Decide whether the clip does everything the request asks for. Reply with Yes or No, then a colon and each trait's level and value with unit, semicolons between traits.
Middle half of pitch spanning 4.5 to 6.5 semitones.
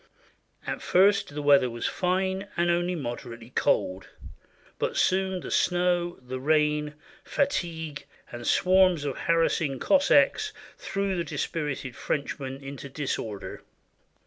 Yes: average, 5.2 semitones